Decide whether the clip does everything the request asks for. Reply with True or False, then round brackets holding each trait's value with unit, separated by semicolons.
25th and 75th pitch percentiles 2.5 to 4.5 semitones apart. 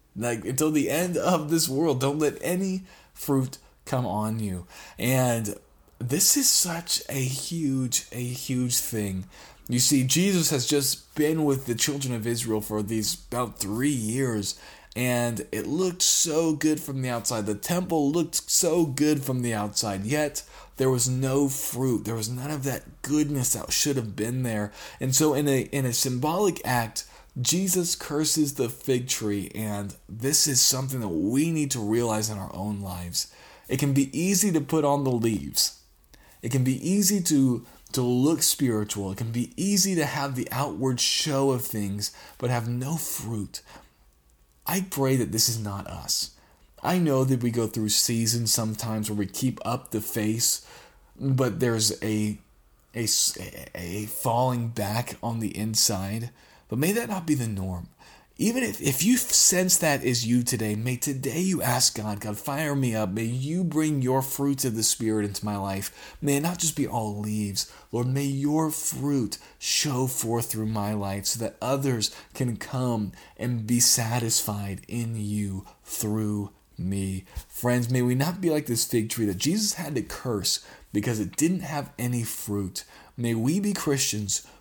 False (5.0 semitones)